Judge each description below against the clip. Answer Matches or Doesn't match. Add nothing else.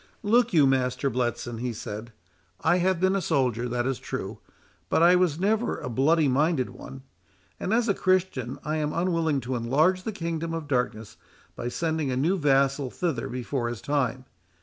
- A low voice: Doesn't match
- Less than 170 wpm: Doesn't match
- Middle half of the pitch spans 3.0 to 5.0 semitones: Doesn't match